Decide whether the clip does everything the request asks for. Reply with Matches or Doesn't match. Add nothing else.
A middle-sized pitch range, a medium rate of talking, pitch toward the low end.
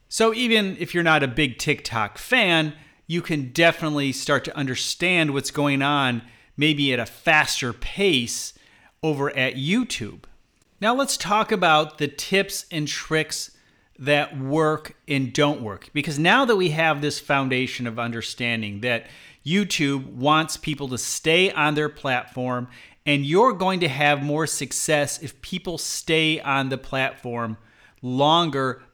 Doesn't match